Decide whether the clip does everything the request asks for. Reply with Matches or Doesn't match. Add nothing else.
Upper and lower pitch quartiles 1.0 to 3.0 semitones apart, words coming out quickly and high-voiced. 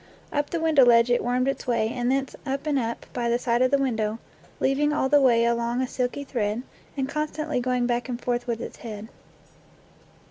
Matches